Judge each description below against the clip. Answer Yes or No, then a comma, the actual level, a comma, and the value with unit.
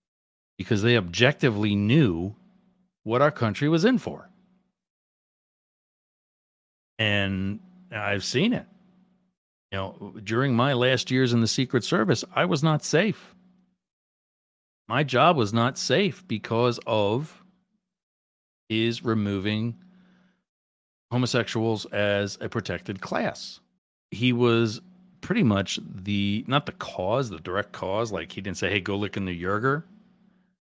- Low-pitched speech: Yes, low, 115 Hz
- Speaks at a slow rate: Yes, slow, 125 wpm